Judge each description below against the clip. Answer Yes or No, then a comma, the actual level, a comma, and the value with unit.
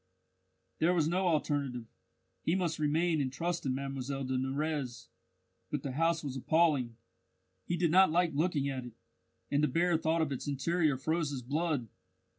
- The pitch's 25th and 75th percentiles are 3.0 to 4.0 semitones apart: Yes, average, 3.6 semitones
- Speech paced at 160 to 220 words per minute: Yes, average, 170 wpm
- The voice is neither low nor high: Yes, medium, 150 Hz